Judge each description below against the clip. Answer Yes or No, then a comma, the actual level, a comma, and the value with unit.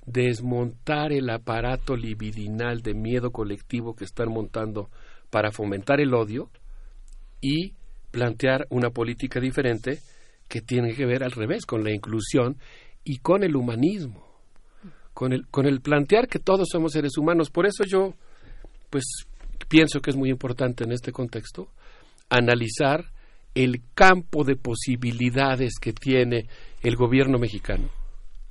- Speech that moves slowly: No, average, 135 wpm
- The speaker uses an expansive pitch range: No, average, 3.5 semitones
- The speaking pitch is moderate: No, low, 125 Hz